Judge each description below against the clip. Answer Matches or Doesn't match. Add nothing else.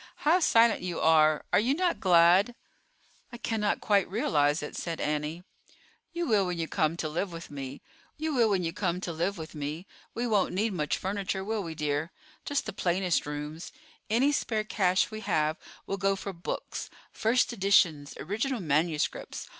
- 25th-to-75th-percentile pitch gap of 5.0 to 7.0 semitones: Matches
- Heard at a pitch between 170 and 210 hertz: Matches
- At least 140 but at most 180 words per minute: Matches